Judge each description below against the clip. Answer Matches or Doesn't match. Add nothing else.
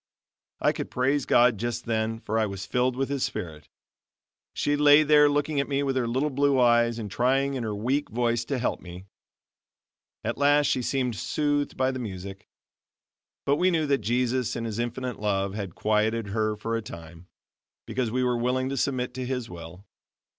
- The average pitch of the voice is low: Matches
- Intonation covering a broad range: Doesn't match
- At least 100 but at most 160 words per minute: Doesn't match